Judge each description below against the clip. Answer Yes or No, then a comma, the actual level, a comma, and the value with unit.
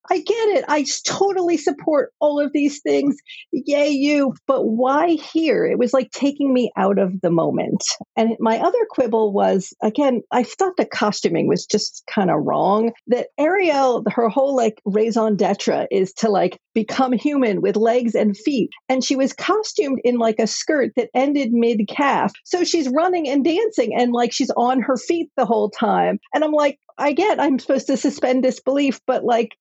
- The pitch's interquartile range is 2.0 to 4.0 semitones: No, average, 4.5 semitones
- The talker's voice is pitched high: Yes, very high, 260 Hz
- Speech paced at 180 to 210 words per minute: Yes, average, 185 wpm